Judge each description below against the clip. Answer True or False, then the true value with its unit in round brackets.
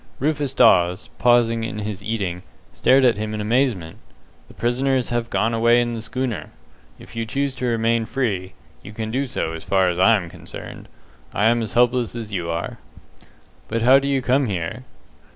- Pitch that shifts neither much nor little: True (3.4 semitones)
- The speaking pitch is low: True (115 Hz)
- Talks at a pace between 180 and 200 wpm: True (190 wpm)